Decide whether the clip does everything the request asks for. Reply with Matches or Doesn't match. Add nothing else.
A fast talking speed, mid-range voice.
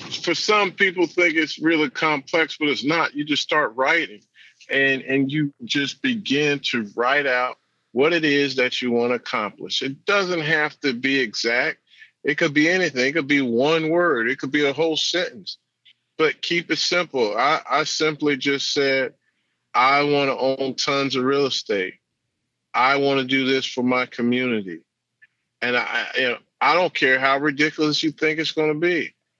Doesn't match